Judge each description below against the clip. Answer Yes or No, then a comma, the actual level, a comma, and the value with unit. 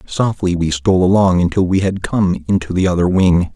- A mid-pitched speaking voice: No, very low, 90 Hz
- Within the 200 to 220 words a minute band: Yes, fast, 205 wpm